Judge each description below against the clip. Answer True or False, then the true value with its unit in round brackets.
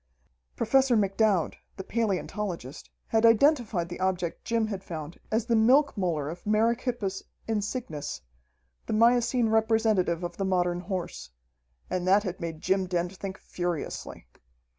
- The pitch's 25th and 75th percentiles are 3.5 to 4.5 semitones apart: True (4.2 semitones)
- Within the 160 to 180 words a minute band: False (135 wpm)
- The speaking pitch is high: True (195 Hz)